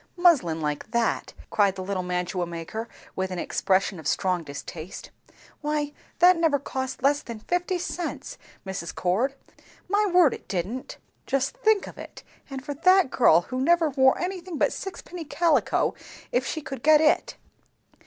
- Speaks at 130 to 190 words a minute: Yes, average, 160 wpm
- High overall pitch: Yes, very high, 265 Hz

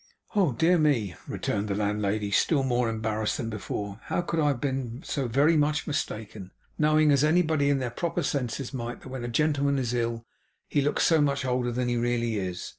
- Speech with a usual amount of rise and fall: Yes, average, 4.5 semitones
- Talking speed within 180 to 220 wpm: Yes, average, 195 wpm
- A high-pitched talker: No, low, 125 Hz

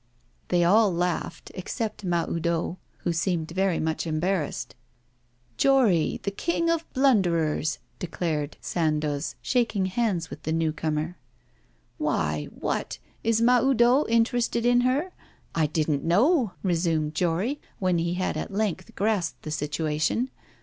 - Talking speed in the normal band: No, slow, 125 wpm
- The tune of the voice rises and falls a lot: Yes, wide, 6.1 semitones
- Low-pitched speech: No, medium, 180 Hz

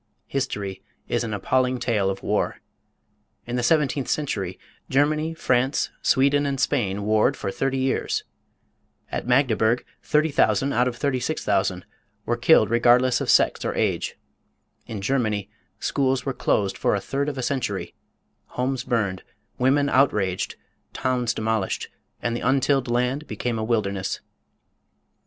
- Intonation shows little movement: No, average, 3.9 semitones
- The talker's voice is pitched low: Yes, low, 125 Hz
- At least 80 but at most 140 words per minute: Yes, slow, 135 wpm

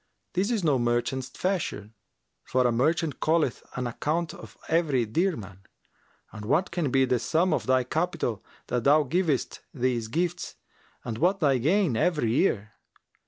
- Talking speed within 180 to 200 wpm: No, average, 155 wpm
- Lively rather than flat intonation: Yes, wide, 5.9 semitones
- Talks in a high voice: No, medium, 140 Hz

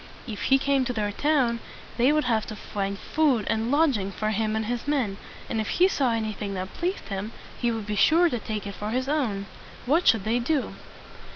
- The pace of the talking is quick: Yes, fast, 220 wpm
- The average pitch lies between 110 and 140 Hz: No, high, 230 Hz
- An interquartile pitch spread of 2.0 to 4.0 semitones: No, average, 4.7 semitones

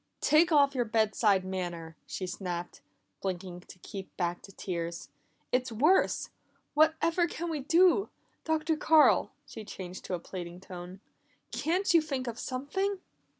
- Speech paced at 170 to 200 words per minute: No, average, 150 wpm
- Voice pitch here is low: No, high, 225 Hz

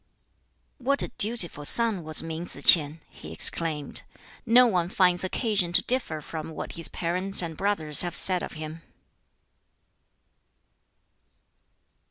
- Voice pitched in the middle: Yes, medium, 175 Hz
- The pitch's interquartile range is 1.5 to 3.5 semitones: No, average, 4.0 semitones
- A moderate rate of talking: No, slow, 130 wpm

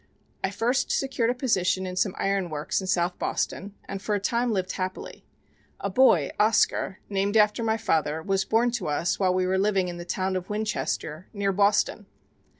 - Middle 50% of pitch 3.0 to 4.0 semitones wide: No, narrow, 2.6 semitones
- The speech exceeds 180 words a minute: Yes, average, 190 wpm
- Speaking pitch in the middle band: No, high, 195 Hz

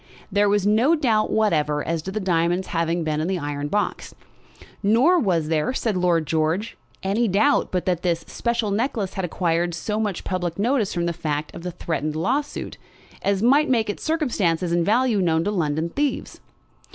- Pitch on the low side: No, medium, 185 Hz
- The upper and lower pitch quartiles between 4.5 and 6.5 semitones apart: Yes, average, 4.8 semitones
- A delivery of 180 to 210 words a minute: Yes, average, 185 wpm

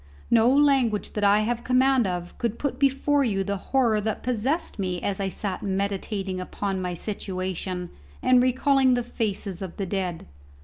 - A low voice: No, high, 210 Hz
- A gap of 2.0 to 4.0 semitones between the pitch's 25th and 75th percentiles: No, average, 4.8 semitones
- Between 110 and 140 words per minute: No, average, 170 wpm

